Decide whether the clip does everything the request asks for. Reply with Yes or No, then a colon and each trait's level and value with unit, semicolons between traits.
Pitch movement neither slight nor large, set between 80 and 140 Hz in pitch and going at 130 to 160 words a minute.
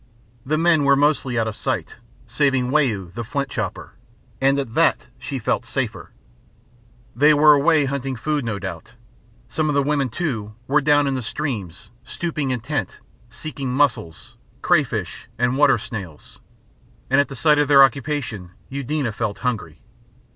Yes: average, 4.2 semitones; low, 135 Hz; average, 155 wpm